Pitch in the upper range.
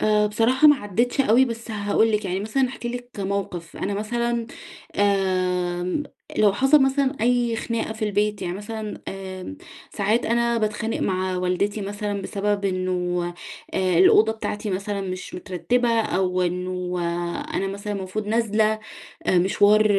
Yes: high, 205 Hz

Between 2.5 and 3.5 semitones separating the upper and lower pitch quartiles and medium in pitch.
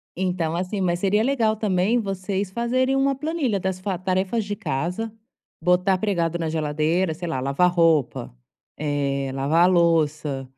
No: average, 4.3 semitones; medium, 180 Hz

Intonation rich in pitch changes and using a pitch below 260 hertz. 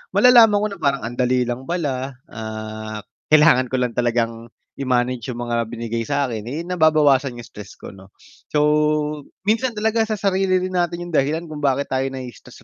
Yes: wide, 6.3 semitones; low, 135 Hz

